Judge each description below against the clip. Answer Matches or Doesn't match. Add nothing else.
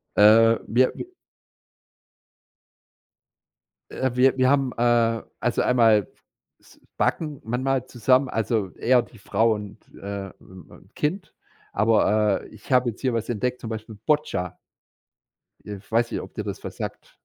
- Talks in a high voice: Doesn't match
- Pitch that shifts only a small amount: Doesn't match